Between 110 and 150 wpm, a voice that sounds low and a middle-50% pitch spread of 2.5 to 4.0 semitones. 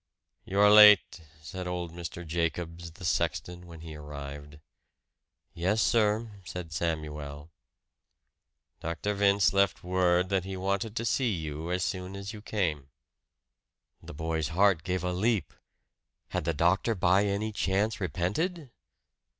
Yes: slow, 135 wpm; very low, 90 Hz; average, 3.4 semitones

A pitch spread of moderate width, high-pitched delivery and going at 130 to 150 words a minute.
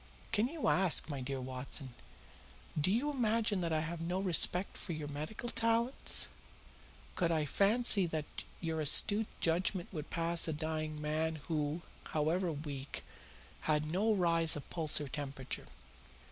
No: average, 4.2 semitones; medium, 165 Hz; average, 145 wpm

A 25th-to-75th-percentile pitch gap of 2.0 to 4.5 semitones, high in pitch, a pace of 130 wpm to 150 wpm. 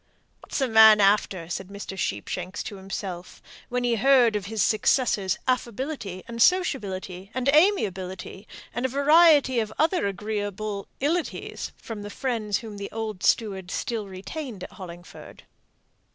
No: average, 4.9 semitones; high, 215 Hz; average, 140 wpm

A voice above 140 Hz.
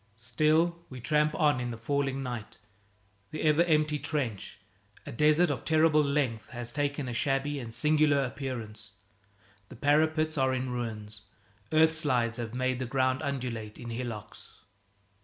No: low, 135 Hz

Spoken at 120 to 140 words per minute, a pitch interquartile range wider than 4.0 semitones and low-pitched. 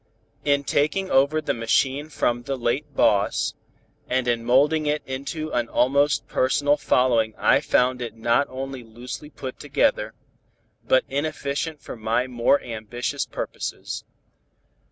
No: slow, 135 wpm; average, 3.2 semitones; low, 130 Hz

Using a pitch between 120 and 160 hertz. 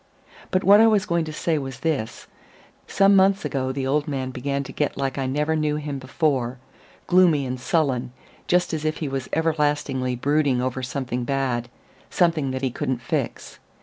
Yes: medium, 140 Hz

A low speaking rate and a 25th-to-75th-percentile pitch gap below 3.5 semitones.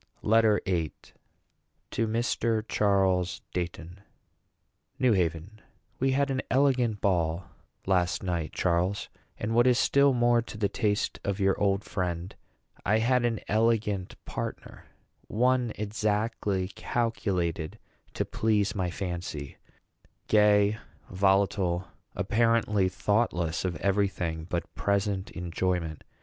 No: slow, 115 wpm; average, 3.8 semitones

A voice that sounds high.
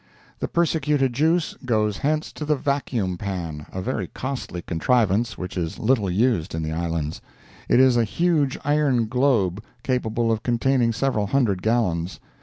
No: low, 115 Hz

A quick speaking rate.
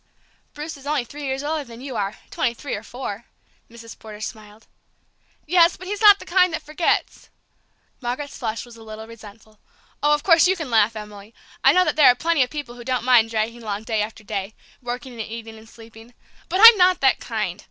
Yes: fast, 215 wpm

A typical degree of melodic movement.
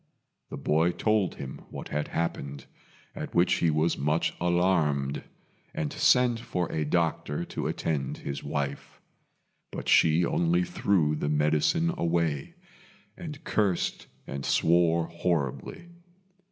Yes: average, 3.6 semitones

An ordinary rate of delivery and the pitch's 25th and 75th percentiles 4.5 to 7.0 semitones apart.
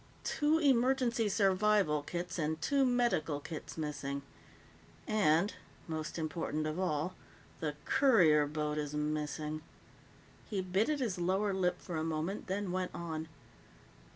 No: slow, 130 wpm; average, 5.2 semitones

